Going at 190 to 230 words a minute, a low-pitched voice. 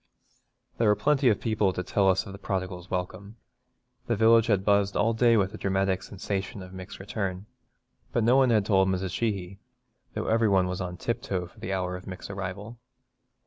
Yes: average, 195 wpm; low, 100 Hz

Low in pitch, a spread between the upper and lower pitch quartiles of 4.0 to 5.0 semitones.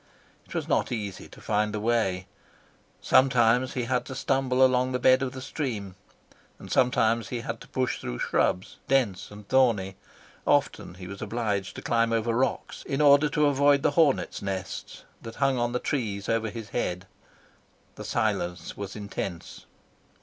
Yes: low, 115 Hz; average, 4.4 semitones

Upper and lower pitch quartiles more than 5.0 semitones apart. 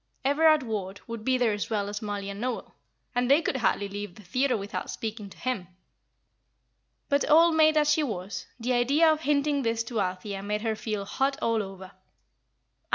Yes: wide, 5.4 semitones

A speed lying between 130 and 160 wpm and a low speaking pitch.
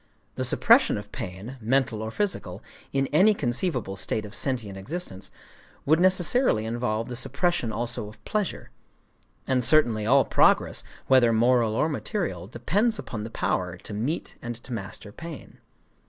Yes: average, 140 wpm; low, 120 Hz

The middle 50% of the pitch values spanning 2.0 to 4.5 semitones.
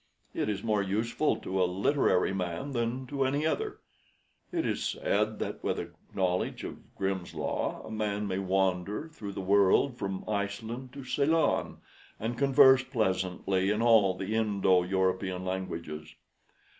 No: average, 5.2 semitones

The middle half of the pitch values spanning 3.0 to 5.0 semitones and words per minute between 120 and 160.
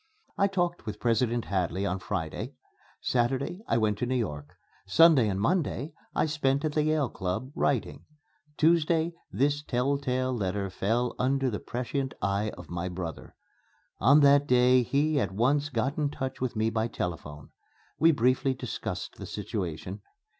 No: wide, 5.5 semitones; average, 155 wpm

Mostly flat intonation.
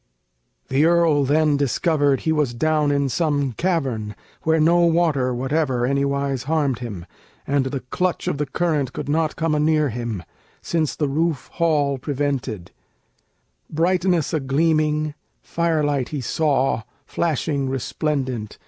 No: average, 3.1 semitones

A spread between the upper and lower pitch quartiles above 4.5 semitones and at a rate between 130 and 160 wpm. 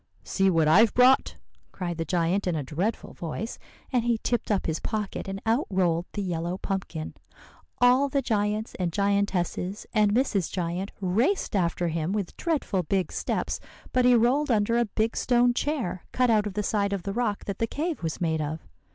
No: average, 4.9 semitones; average, 190 wpm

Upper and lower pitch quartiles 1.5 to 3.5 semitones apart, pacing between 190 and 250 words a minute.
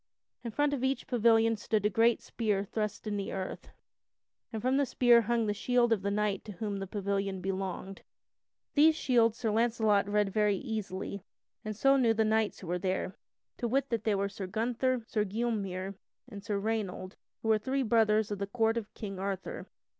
Yes: average, 2.8 semitones; average, 195 wpm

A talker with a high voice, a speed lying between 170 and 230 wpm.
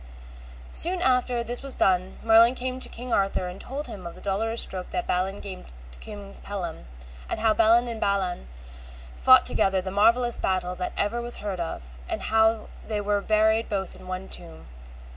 Yes: high, 205 Hz; average, 185 wpm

